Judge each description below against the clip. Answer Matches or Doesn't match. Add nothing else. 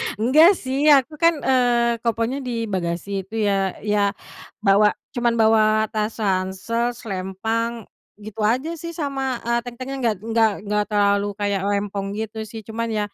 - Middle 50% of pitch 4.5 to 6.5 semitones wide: Doesn't match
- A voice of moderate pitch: Doesn't match